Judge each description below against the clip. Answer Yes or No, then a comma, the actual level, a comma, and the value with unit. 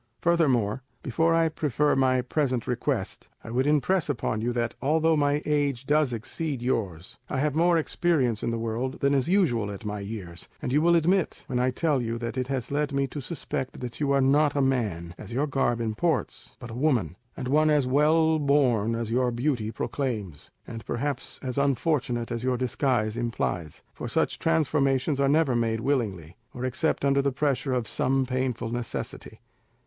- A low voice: Yes, low, 130 Hz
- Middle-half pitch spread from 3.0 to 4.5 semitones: Yes, average, 4.0 semitones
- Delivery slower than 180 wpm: No, average, 185 wpm